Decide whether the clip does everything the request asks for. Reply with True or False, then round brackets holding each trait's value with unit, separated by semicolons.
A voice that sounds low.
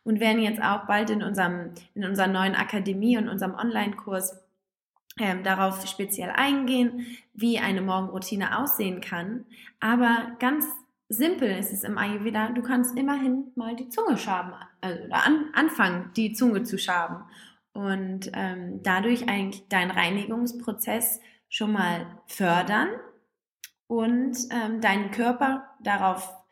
False (215 Hz)